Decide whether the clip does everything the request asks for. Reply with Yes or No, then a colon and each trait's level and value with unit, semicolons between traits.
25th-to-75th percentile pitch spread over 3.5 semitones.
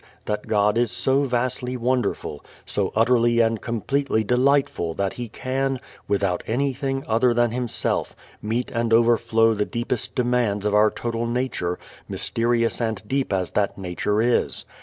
No: average, 2.8 semitones